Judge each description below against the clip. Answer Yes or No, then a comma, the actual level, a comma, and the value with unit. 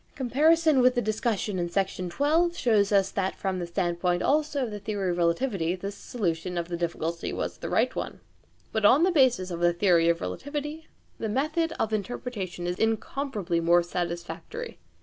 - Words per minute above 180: No, average, 175 wpm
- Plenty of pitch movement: Yes, wide, 7.1 semitones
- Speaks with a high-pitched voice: Yes, high, 200 Hz